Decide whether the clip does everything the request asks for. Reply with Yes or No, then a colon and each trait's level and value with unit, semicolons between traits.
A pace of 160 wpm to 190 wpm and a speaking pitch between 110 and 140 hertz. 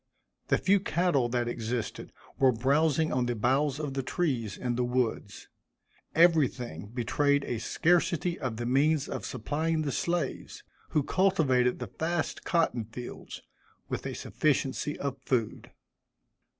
No: slow, 135 wpm; low, 135 Hz